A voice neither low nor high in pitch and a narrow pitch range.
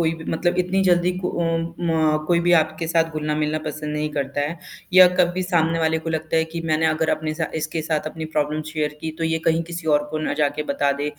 Yes: medium, 160 Hz; narrow, 1.5 semitones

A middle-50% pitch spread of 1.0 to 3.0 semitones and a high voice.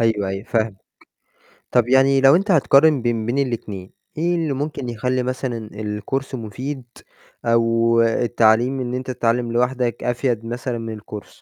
No: narrow, 2.6 semitones; low, 120 Hz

